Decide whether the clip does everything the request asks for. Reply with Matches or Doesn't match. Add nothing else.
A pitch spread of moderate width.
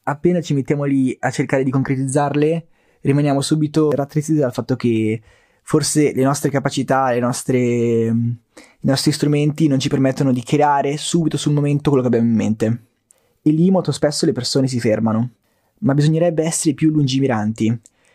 Matches